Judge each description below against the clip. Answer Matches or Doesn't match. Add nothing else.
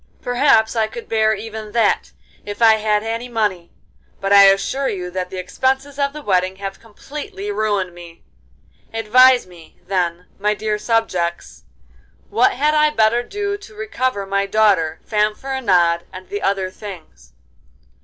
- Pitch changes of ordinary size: Matches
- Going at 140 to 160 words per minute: Matches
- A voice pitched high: Matches